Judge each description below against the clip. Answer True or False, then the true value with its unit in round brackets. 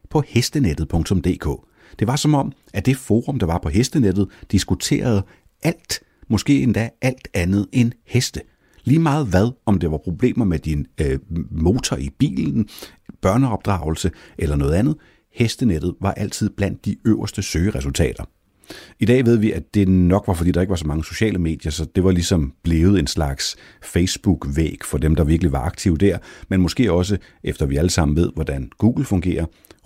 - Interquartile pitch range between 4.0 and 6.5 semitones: True (5.1 semitones)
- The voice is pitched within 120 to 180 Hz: False (95 Hz)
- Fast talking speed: False (175 wpm)